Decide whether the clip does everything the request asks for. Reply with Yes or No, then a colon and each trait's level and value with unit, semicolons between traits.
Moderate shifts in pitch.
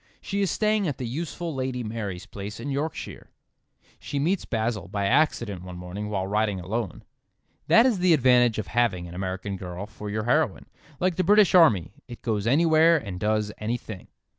No: wide, 7.6 semitones